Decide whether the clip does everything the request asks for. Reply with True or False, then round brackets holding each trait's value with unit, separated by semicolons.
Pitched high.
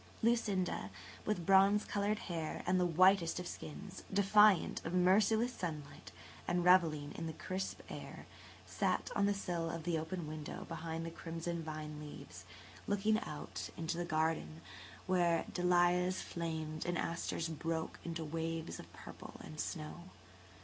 False (170 Hz)